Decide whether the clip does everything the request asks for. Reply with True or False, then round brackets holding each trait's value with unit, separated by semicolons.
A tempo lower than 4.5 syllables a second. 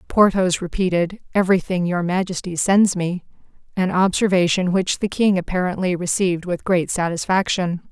False (5.1 syllables/s)